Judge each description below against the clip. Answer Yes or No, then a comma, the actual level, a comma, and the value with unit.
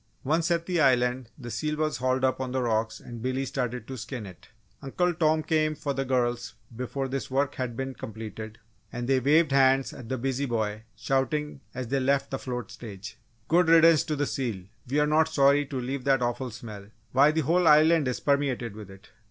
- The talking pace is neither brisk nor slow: No, fast, 210 wpm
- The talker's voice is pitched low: Yes, low, 130 Hz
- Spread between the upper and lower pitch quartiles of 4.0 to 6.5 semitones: No, average, 3.5 semitones